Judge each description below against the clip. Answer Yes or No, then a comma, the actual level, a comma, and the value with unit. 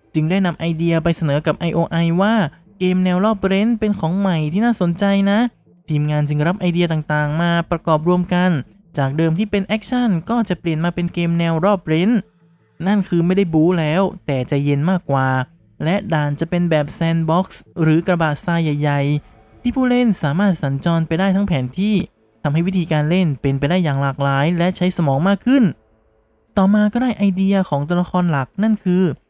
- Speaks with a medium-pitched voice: Yes, medium, 170 Hz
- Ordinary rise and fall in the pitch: Yes, average, 4.1 semitones